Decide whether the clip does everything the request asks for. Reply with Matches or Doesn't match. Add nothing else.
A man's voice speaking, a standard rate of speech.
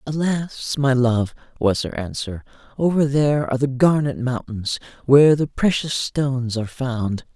Matches